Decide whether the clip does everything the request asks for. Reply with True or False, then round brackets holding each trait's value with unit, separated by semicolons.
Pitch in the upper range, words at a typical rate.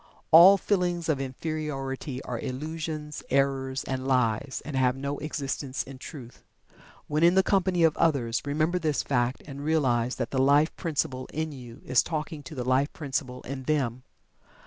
False (140 Hz; 165 wpm)